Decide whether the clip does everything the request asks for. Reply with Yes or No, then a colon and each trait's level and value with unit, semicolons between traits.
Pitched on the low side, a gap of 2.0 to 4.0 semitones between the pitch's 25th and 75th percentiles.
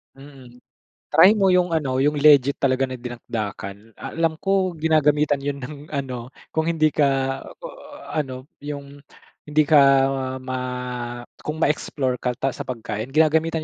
No: medium, 145 Hz; average, 3.4 semitones